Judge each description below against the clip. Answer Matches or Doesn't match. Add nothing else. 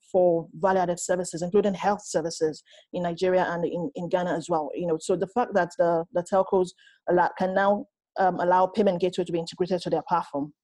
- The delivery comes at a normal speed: Matches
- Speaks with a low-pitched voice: Doesn't match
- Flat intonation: Matches